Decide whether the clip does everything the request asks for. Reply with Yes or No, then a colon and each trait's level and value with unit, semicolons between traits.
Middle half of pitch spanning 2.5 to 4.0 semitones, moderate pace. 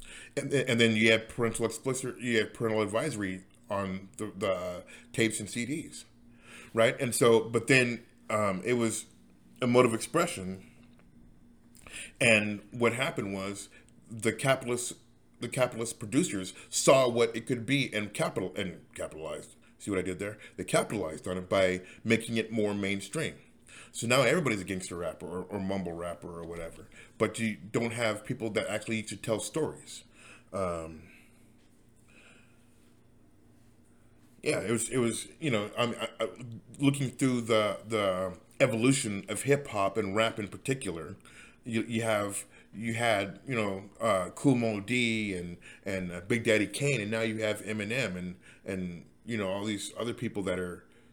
Yes: average, 3.2 semitones; average, 160 wpm